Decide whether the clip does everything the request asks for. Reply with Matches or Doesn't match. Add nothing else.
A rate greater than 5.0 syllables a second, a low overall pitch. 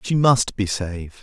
Doesn't match